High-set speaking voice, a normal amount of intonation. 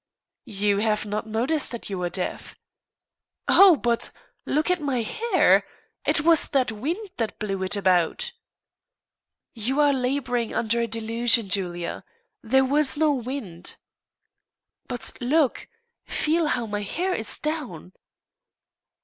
No: high, 240 Hz; wide, 5.9 semitones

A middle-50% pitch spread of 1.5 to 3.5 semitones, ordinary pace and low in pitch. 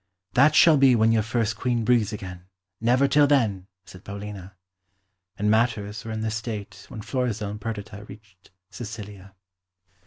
Yes: average, 2.8 semitones; average, 155 wpm; low, 110 Hz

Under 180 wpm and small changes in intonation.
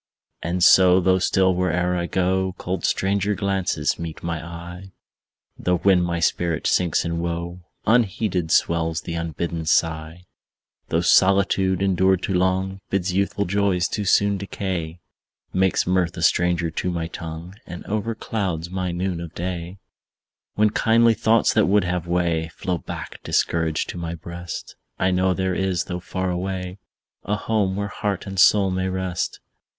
Yes: average, 155 wpm; narrow, 2.0 semitones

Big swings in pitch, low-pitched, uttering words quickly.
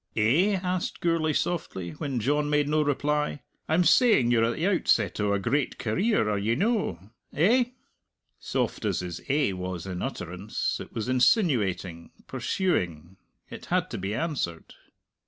No: wide, 8.7 semitones; low, 130 Hz; average, 155 wpm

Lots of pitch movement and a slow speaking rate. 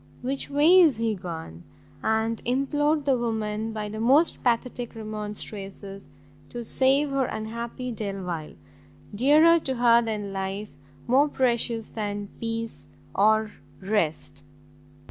No: average, 3.9 semitones; slow, 120 wpm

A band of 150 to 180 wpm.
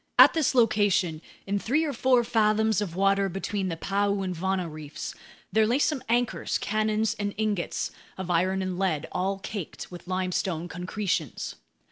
Yes: average, 160 wpm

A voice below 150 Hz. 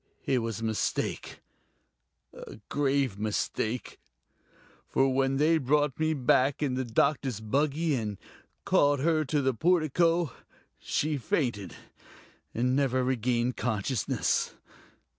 Yes: low, 135 Hz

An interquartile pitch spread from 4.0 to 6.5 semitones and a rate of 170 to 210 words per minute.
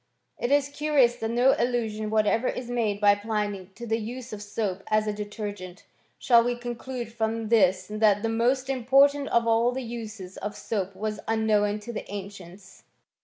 No: narrow, 2.6 semitones; average, 185 wpm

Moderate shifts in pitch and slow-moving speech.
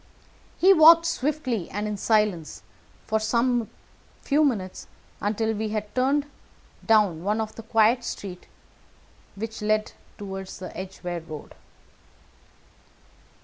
Yes: average, 3.7 semitones; slow, 115 wpm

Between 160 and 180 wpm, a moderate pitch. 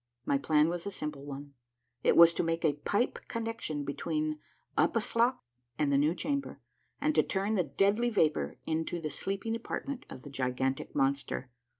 Yes: average, 170 wpm; medium, 160 Hz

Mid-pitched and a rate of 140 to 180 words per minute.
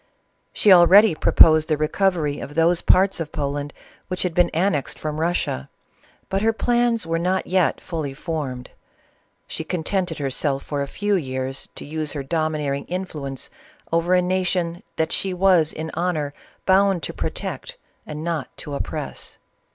Yes: medium, 165 Hz; average, 155 wpm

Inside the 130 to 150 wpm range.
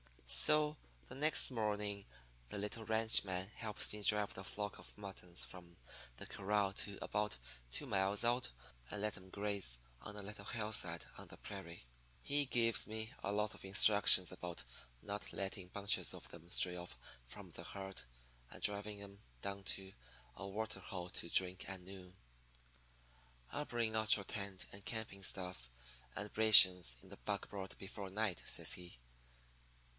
No: average, 160 wpm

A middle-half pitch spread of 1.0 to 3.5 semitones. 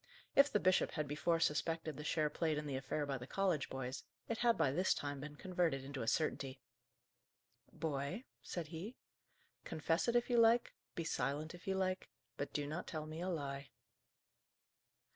No: average, 4.2 semitones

